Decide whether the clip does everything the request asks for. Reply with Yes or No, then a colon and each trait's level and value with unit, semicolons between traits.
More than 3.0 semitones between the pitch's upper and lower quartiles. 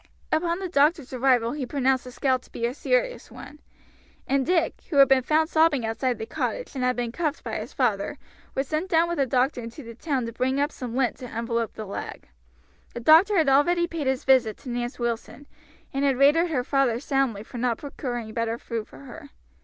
Yes: average, 4.1 semitones